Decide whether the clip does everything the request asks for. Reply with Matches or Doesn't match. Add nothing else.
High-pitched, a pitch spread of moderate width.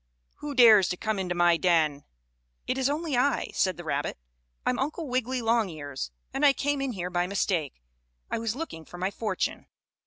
Doesn't match